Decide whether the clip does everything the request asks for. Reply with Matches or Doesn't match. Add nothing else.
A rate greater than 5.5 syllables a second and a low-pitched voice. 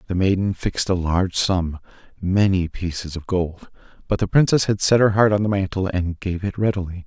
Doesn't match